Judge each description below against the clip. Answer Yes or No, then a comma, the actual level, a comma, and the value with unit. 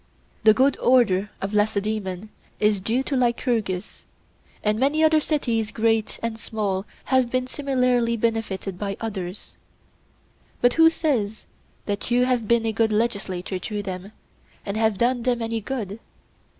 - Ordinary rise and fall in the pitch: Yes, average, 3.3 semitones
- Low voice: No, high, 225 Hz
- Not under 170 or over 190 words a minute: No, average, 145 wpm